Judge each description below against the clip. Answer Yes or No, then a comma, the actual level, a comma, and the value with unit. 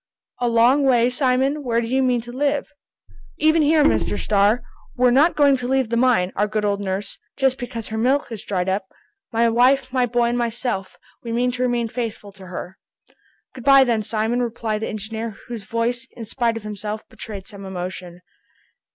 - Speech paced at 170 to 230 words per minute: Yes, average, 195 wpm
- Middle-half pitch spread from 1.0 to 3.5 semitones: Yes, average, 3.1 semitones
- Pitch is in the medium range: No, high, 235 Hz